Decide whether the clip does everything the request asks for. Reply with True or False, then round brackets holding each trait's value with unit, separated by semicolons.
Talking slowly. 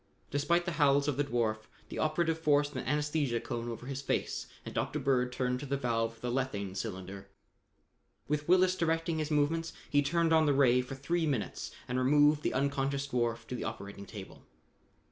False (190 wpm)